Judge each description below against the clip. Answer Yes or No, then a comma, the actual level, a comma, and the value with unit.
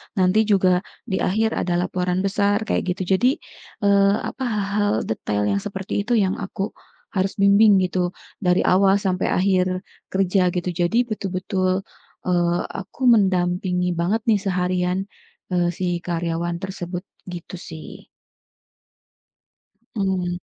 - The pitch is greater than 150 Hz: Yes, medium, 185 Hz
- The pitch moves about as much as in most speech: No, narrow, 2.0 semitones